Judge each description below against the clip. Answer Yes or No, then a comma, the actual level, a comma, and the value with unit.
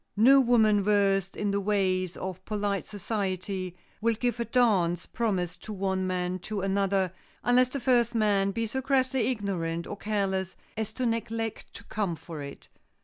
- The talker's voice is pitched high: Yes, high, 205 Hz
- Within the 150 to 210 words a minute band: Yes, average, 165 wpm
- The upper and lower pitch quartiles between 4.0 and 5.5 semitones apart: No, average, 3.4 semitones